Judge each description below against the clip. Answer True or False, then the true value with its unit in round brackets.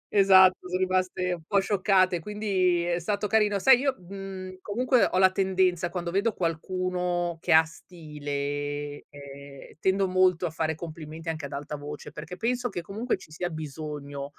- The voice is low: False (180 Hz)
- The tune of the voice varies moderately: True (3.4 semitones)